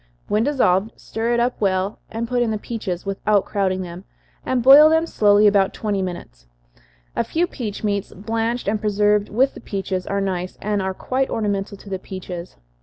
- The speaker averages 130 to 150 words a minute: No, average, 185 wpm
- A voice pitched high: Yes, high, 205 Hz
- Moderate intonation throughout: Yes, average, 3.2 semitones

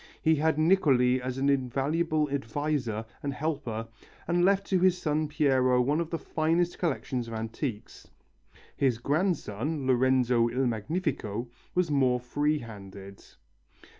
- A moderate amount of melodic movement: Yes, average, 4.4 semitones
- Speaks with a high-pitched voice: No, medium, 140 Hz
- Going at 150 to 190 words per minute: No, slow, 135 wpm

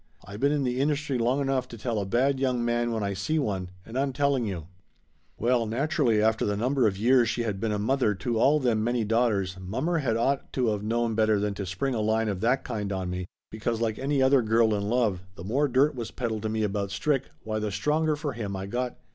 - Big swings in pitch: No, average, 3.9 semitones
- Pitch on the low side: Yes, low, 115 Hz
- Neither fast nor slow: No, fast, 250 wpm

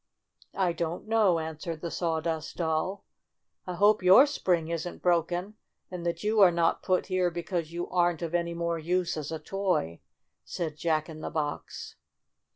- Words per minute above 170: No, average, 165 wpm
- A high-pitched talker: No, medium, 170 Hz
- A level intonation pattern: Yes, narrow, 2.1 semitones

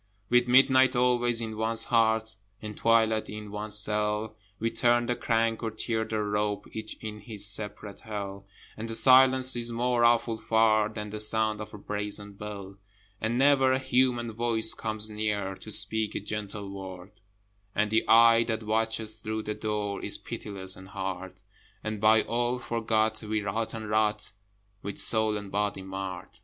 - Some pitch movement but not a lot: No, narrow, 1.6 semitones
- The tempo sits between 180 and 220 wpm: No, average, 170 wpm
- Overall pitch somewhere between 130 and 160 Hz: No, low, 110 Hz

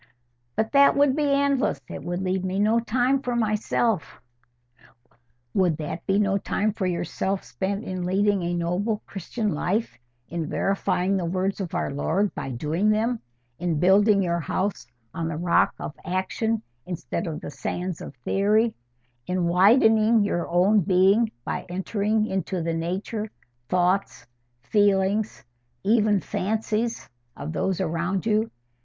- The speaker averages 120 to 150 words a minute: Yes, average, 145 wpm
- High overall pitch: Yes, high, 195 Hz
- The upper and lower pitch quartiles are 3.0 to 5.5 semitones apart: Yes, average, 3.5 semitones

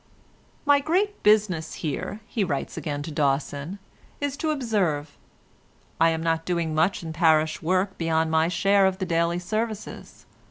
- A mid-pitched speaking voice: Yes, medium, 170 Hz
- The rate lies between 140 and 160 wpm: Yes, average, 155 wpm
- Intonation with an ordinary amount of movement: Yes, average, 4.4 semitones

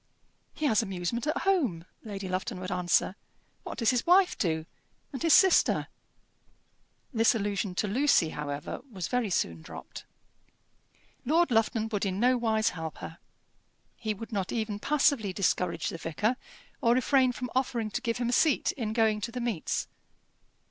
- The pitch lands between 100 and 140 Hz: No, high, 220 Hz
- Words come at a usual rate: Yes, average, 160 wpm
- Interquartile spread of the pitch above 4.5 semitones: Yes, average, 5.0 semitones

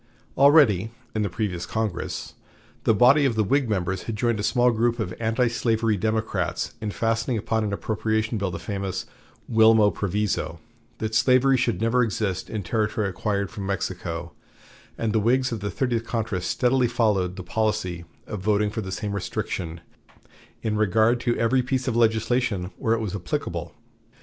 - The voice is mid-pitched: No, low, 110 Hz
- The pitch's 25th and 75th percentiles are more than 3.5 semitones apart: No, average, 2.7 semitones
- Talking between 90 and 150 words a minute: No, average, 165 wpm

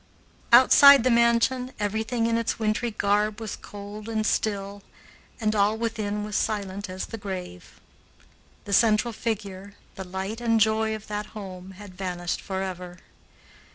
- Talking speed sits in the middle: Yes, average, 145 wpm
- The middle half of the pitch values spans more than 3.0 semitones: No, narrow, 2.4 semitones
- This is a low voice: No, high, 210 Hz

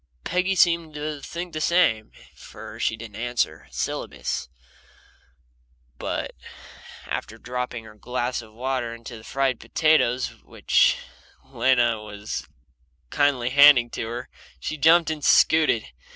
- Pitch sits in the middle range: No, low, 125 Hz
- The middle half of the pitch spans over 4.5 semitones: Yes, average, 4.9 semitones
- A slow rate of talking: Yes, slow, 125 wpm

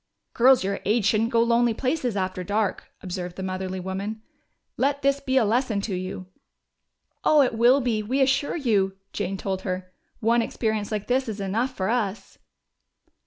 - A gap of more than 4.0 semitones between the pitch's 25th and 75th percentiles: Yes, average, 4.5 semitones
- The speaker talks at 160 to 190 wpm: Yes, average, 170 wpm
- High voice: Yes, high, 220 Hz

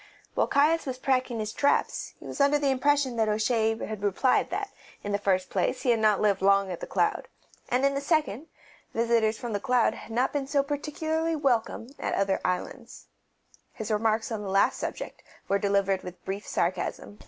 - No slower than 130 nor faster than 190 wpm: No, average, 200 wpm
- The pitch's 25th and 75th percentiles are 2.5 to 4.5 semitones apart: No, average, 5.2 semitones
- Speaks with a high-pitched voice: Yes, high, 225 Hz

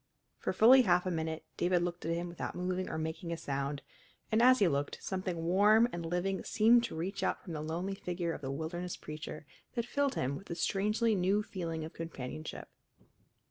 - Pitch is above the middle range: No, medium, 175 Hz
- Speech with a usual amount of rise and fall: Yes, average, 3.5 semitones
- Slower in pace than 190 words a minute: No, average, 200 wpm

